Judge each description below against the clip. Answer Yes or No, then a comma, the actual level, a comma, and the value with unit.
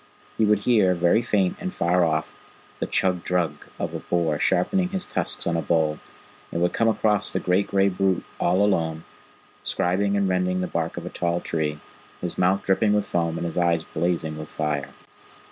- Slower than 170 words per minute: No, average, 195 wpm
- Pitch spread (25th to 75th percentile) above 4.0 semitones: No, average, 3.1 semitones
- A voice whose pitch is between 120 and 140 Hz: No, very low, 90 Hz